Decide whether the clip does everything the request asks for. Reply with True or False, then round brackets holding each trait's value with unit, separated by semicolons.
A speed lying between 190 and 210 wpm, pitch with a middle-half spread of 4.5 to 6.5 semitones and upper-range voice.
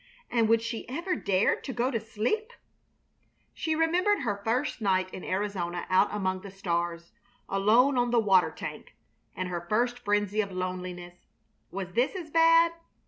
False (160 wpm; 5.2 semitones; 210 Hz)